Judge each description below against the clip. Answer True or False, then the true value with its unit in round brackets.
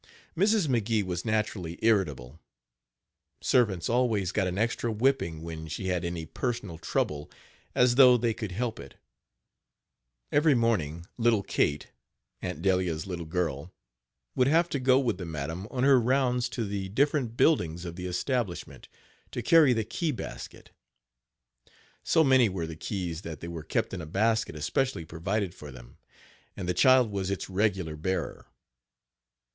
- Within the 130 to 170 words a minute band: True (155 wpm)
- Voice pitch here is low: True (100 Hz)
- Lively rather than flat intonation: True (6.4 semitones)